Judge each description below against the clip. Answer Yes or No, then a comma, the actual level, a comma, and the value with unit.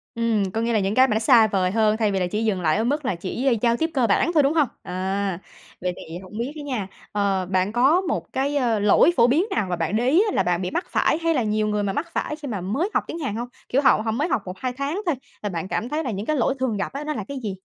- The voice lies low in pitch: No, high, 225 Hz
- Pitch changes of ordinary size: No, wide, 5.8 semitones